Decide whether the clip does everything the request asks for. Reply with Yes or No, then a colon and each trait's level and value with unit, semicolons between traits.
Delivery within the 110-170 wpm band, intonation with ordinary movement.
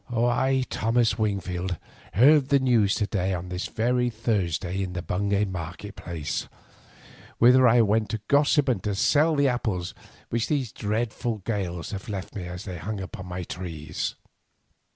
Yes: average, 160 wpm; average, 4.8 semitones